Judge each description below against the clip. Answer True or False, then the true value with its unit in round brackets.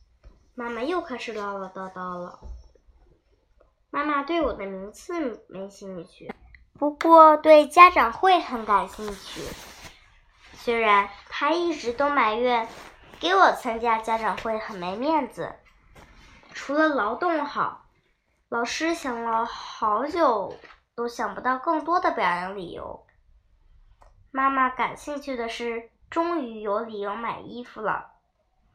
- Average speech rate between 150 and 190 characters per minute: True (185 characters per minute)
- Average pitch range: False (6.2 semitones)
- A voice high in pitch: True (240 Hz)